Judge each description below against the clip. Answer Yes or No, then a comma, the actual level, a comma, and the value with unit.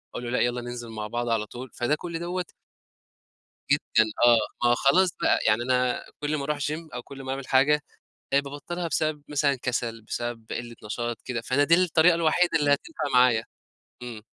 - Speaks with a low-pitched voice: Yes, low, 130 Hz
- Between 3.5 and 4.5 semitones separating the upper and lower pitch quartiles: Yes, average, 4.0 semitones